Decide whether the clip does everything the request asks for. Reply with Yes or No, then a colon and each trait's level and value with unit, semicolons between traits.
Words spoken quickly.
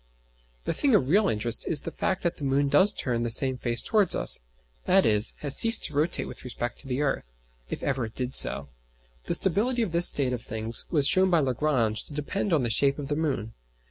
Yes: fast, 225 wpm